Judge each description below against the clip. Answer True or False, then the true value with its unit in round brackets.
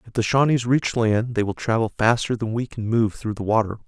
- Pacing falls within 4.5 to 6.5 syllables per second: True (5.5 syllables/s)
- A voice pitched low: True (115 Hz)